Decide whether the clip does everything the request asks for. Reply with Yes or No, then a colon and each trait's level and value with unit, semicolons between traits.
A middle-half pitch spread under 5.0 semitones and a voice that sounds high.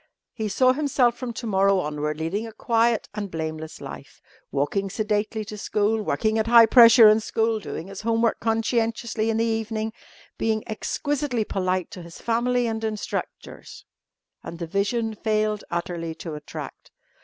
Yes: narrow, 2.6 semitones; high, 220 Hz